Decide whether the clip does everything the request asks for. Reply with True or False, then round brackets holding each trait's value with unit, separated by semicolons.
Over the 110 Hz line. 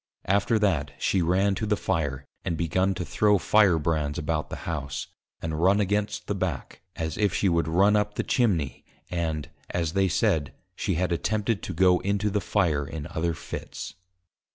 False (90 Hz)